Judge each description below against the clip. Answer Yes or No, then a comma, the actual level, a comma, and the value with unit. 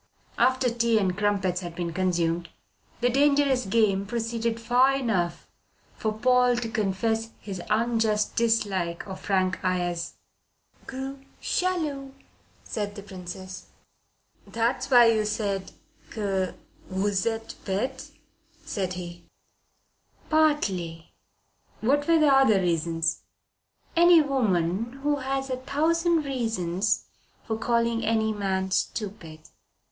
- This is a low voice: No, high, 220 Hz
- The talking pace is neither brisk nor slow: No, slow, 110 wpm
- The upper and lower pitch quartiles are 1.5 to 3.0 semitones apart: No, average, 5.1 semitones